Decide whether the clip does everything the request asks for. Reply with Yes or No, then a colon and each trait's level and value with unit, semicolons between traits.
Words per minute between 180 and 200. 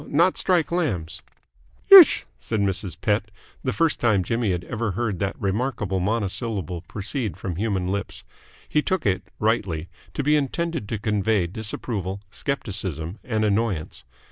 No: average, 145 wpm